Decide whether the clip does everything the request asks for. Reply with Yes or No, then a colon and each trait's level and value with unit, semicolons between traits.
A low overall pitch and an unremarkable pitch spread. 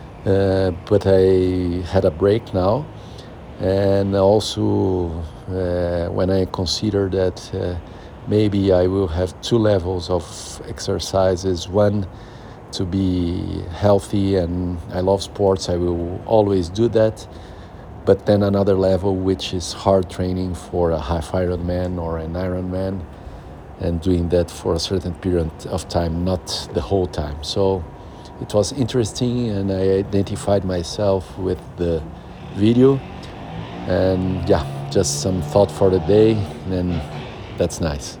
No: very low, 95 Hz; narrow, 2.0 semitones